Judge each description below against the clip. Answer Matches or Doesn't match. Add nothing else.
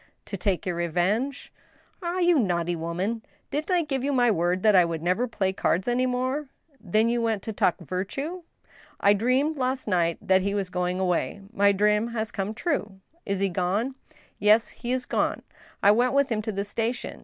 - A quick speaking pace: Matches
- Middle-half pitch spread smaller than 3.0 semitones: Doesn't match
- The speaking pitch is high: Matches